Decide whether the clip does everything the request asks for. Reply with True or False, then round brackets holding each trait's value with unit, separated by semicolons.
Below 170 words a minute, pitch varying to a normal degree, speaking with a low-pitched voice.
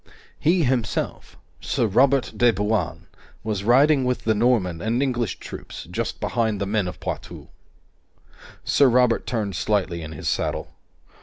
True (145 wpm; 3.8 semitones; 115 Hz)